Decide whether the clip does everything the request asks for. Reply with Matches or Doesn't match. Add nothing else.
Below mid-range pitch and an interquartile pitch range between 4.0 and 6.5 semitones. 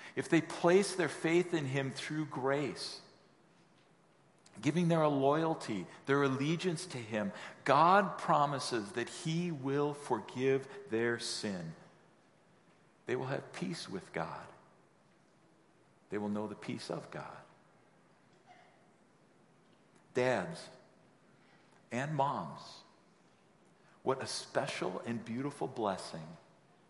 Doesn't match